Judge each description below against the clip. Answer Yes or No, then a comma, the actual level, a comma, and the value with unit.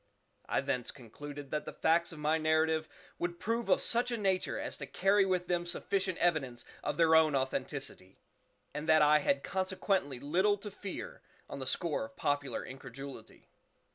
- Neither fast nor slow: Yes, average, 170 wpm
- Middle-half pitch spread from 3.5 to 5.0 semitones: Yes, average, 4.7 semitones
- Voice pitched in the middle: Yes, medium, 160 Hz